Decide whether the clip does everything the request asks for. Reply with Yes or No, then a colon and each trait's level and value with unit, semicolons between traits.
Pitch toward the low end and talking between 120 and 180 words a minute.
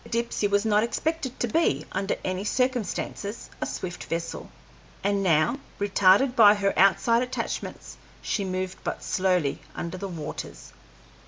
No: high, 200 Hz; average, 145 wpm